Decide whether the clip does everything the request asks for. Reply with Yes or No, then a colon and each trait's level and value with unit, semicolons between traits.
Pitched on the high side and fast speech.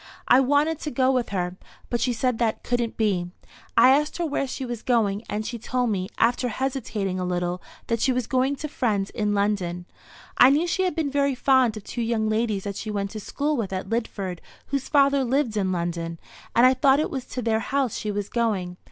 Yes: high, 235 Hz; fast, 220 wpm